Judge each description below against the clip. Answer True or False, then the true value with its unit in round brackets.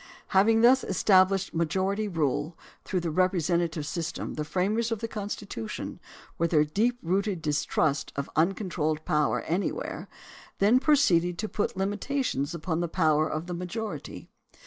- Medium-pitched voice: True (180 Hz)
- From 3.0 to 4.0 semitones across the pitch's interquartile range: False (4.5 semitones)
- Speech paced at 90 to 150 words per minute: True (145 wpm)